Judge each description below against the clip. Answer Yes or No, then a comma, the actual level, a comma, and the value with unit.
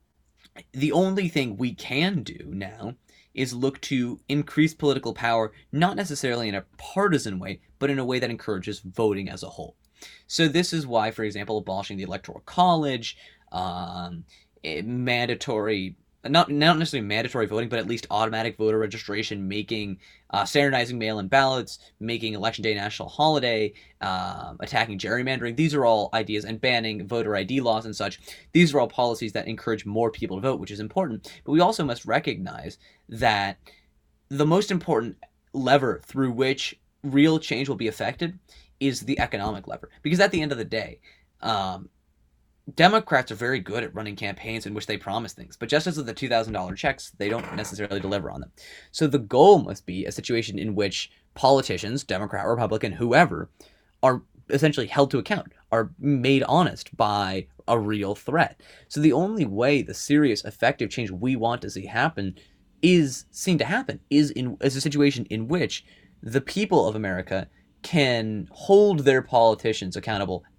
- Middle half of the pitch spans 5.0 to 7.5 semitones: Yes, wide, 5.6 semitones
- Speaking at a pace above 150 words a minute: Yes, average, 170 wpm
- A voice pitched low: Yes, low, 115 Hz